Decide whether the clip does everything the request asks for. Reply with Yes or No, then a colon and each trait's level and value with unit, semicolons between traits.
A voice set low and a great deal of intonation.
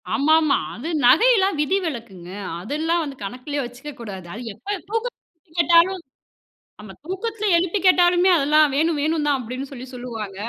No: very high, 300 Hz; wide, 6.2 semitones